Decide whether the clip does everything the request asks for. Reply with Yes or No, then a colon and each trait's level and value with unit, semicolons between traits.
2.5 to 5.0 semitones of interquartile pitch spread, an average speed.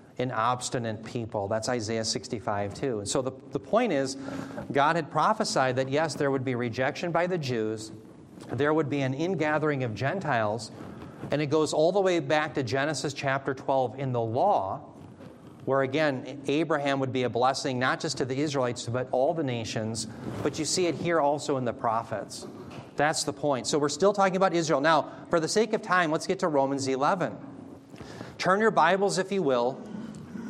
Yes: average, 4.0 semitones; average, 190 wpm